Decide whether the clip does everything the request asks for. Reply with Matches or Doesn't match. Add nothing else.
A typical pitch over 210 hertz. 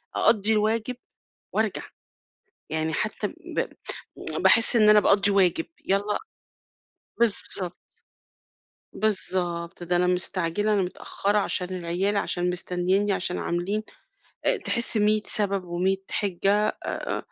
Doesn't match